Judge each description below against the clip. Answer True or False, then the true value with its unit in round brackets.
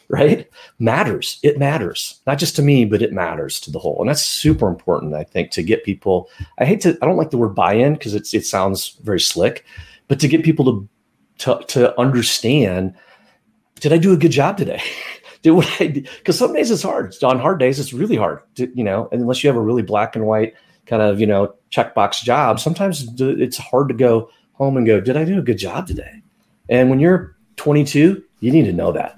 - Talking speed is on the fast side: True (225 wpm)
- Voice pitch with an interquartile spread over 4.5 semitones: True (5.3 semitones)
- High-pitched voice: False (130 Hz)